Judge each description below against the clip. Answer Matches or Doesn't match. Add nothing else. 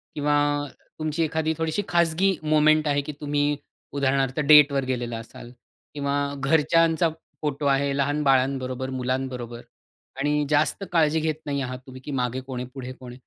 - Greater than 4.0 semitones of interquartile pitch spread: Doesn't match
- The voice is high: Doesn't match